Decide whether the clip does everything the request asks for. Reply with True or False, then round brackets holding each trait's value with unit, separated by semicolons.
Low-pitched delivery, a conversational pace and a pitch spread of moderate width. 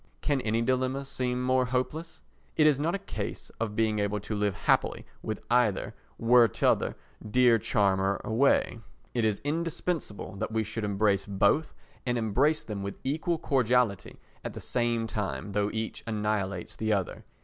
True (115 Hz; 160 wpm; 3.9 semitones)